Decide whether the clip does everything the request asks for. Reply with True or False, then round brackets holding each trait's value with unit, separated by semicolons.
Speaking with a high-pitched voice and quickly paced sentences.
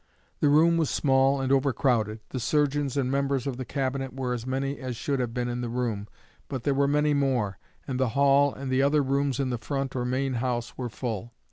False (135 Hz; 220 wpm)